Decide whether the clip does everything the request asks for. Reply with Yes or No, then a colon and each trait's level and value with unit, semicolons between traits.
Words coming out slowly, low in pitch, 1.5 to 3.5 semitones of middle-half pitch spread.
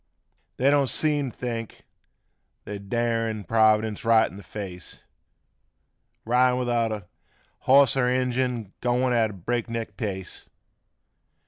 Yes: slow, 130 wpm; low, 115 Hz; average, 2.7 semitones